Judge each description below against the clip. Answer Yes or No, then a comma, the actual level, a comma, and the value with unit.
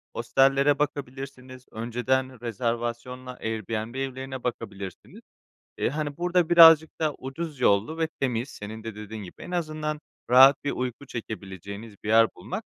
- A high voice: No, low, 130 Hz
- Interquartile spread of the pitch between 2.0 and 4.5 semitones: Yes, average, 4.2 semitones